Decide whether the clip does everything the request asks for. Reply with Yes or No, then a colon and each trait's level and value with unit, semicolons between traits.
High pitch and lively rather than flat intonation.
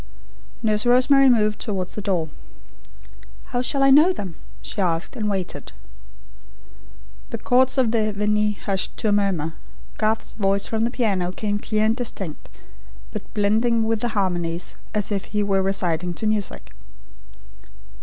No: high, 210 Hz; average, 2.8 semitones